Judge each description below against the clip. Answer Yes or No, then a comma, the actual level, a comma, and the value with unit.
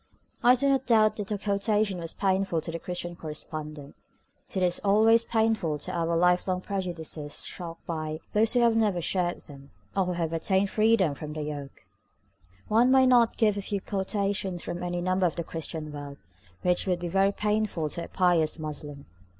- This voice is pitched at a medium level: Yes, medium, 180 Hz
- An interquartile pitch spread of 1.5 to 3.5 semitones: No, average, 4.3 semitones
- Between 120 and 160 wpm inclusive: No, average, 190 wpm